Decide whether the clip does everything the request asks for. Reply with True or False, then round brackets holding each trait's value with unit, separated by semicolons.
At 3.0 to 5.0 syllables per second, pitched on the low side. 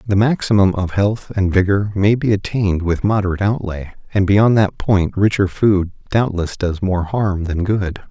True (4.7 syllables/s; 100 Hz)